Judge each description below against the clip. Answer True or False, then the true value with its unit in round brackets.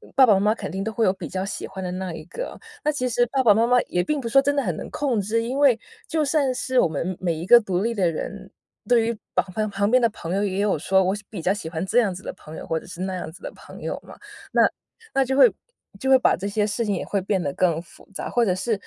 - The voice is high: True (205 Hz)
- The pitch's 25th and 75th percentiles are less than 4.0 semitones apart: False (4.7 semitones)